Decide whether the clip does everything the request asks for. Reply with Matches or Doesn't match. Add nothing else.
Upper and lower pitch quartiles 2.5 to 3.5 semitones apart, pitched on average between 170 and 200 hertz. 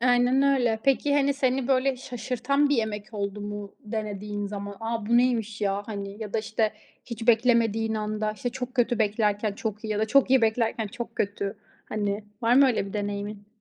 Doesn't match